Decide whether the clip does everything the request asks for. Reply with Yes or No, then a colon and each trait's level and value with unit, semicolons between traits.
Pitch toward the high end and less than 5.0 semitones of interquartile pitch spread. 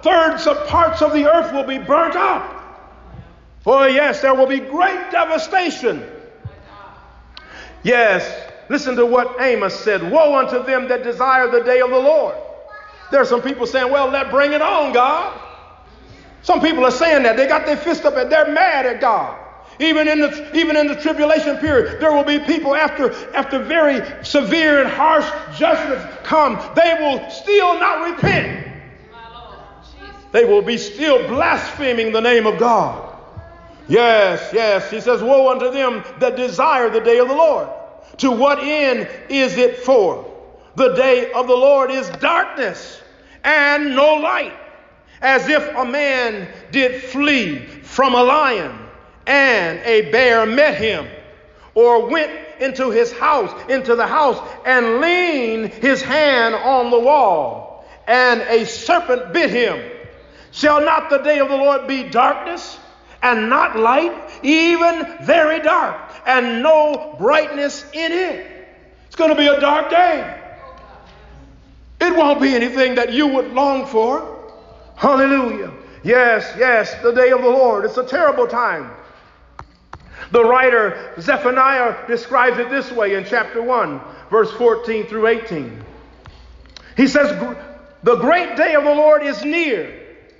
Yes: very high, 280 Hz; average, 3.9 semitones